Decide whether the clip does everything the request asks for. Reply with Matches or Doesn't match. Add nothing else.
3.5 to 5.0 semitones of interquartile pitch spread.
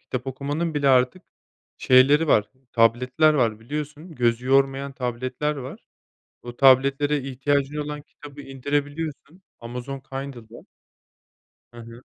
Doesn't match